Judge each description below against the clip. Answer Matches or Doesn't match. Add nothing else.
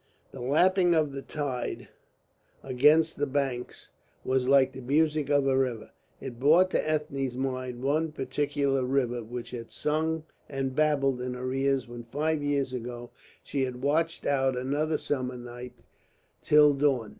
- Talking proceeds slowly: Doesn't match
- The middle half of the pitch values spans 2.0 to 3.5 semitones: Matches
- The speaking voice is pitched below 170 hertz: Matches